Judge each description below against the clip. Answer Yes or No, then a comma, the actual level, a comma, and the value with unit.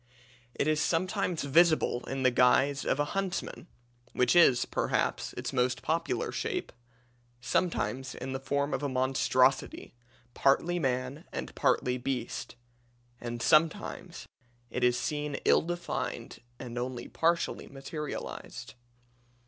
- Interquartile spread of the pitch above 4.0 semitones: Yes, average, 4.4 semitones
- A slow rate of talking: Yes, slow, 125 wpm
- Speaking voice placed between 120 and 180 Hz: Yes, low, 135 Hz